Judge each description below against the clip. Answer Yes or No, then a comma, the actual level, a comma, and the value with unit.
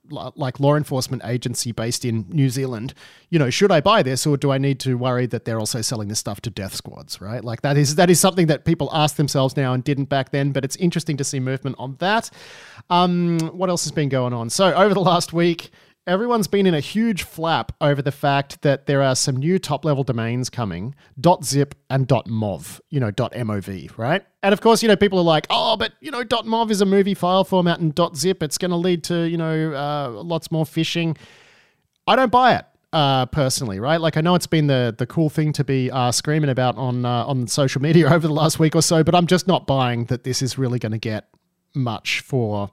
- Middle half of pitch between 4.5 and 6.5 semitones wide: Yes, average, 5.1 semitones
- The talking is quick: Yes, fast, 235 wpm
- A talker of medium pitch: Yes, medium, 145 Hz